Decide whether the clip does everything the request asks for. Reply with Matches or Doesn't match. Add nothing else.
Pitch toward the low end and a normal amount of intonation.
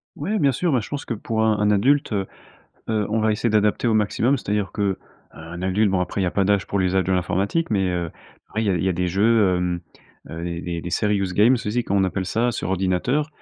Matches